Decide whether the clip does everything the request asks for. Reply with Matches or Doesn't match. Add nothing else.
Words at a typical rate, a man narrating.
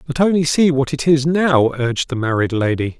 Doesn't match